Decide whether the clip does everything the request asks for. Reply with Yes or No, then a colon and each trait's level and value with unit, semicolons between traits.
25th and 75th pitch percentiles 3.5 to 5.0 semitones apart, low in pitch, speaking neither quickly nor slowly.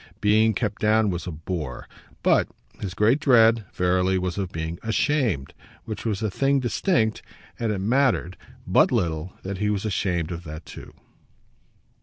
Yes: average, 4.0 semitones; low, 100 Hz; average, 160 wpm